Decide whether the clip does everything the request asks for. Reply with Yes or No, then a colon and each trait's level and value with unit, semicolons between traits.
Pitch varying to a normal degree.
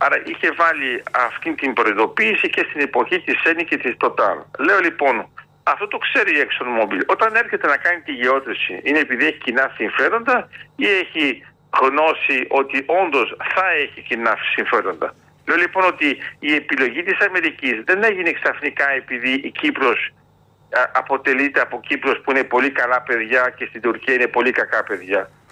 No: wide, 7.1 semitones